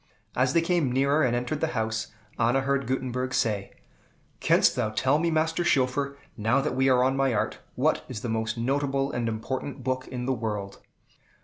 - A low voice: Yes, low, 130 Hz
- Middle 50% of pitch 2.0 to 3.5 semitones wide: Yes, average, 3.1 semitones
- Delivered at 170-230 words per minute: Yes, average, 190 wpm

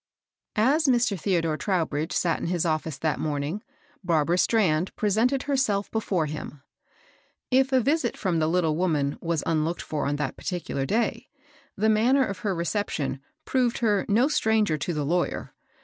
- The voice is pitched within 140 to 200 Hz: Yes, medium, 185 Hz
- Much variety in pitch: Yes, wide, 6.0 semitones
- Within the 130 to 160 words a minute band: No, average, 170 wpm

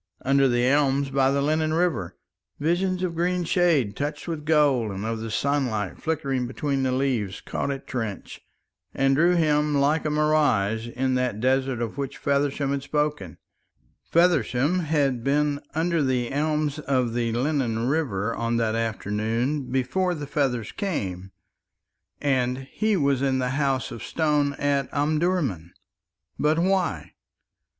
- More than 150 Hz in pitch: No, medium, 140 Hz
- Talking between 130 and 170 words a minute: Yes, average, 150 wpm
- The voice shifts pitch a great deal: No, average, 3.8 semitones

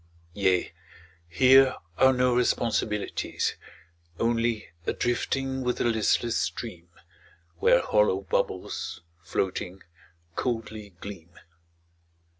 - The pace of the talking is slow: Yes, slow, 85 wpm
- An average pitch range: Yes, average, 4.6 semitones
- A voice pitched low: Yes, low, 110 Hz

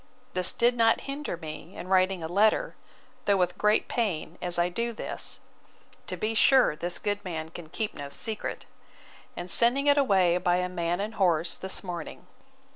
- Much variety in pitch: No, average, 4.2 semitones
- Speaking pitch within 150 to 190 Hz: Yes, medium, 185 Hz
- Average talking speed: Yes, average, 180 wpm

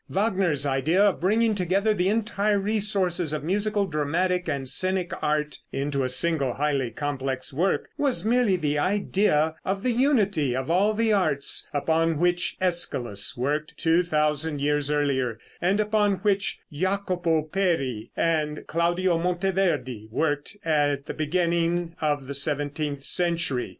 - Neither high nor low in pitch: Yes, medium, 165 Hz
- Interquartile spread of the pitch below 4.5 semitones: No, average, 4.8 semitones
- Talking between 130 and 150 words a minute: Yes, average, 140 wpm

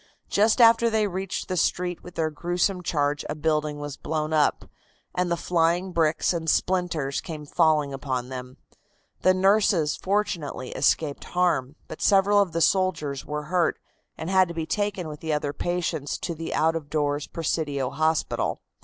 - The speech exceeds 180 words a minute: No, average, 170 wpm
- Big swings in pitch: No, average, 3.4 semitones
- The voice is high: No, medium, 165 Hz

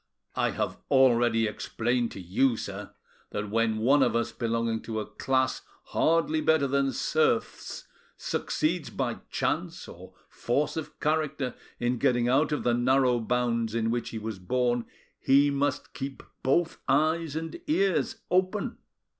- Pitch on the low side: Yes, low, 125 Hz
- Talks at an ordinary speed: Yes, average, 145 wpm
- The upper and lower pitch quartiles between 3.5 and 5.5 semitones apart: Yes, average, 3.9 semitones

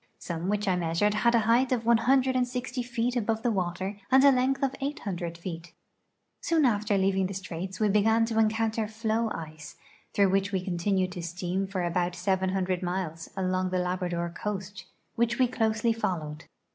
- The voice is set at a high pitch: Yes, high, 200 Hz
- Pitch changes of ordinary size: Yes, average, 4.0 semitones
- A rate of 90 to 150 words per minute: No, average, 170 wpm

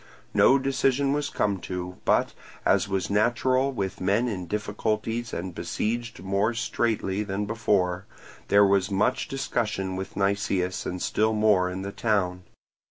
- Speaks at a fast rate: No, average, 145 wpm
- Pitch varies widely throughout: No, average, 3.4 semitones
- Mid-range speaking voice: No, low, 100 Hz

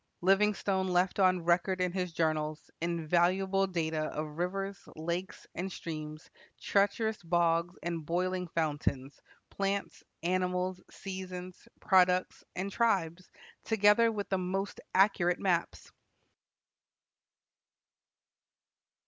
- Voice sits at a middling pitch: Yes, medium, 180 Hz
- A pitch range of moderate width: No, narrow, 2.3 semitones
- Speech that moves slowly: Yes, slow, 100 wpm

